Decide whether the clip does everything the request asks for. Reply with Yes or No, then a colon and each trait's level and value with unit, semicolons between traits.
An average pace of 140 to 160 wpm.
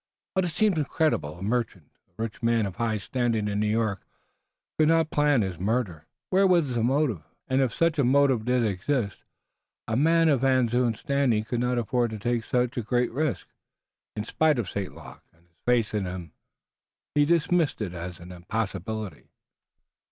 No: average, 185 wpm